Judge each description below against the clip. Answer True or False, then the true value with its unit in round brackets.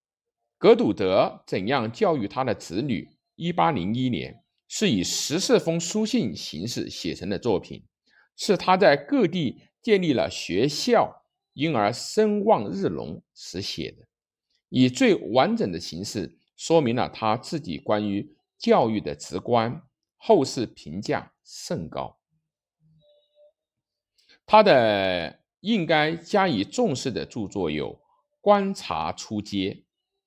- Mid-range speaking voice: True (170 Hz)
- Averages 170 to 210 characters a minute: True (180 characters per minute)